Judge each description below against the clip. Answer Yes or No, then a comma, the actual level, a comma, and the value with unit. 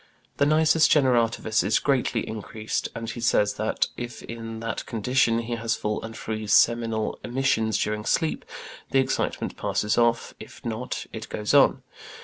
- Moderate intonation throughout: No, narrow, 1.9 semitones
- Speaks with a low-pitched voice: Yes, low, 115 Hz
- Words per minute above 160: No, average, 155 wpm